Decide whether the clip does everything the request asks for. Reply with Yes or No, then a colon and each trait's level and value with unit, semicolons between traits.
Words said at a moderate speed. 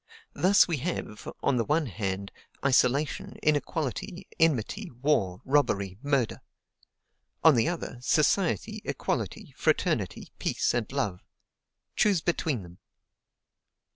No: slow, 105 wpm